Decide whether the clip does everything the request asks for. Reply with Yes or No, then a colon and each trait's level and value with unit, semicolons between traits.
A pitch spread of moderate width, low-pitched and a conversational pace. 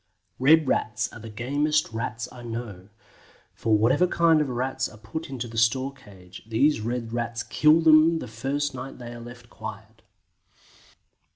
Yes: average, 4.1 semitones; low, 120 Hz; average, 165 wpm